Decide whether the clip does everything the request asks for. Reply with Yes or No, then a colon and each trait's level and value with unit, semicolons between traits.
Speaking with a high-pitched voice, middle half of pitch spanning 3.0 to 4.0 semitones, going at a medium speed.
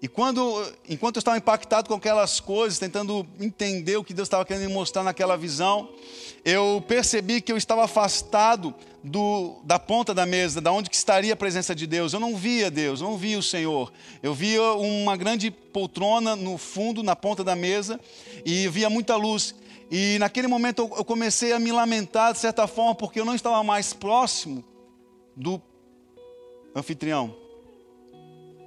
Yes: high, 205 Hz; average, 3.7 semitones; average, 170 wpm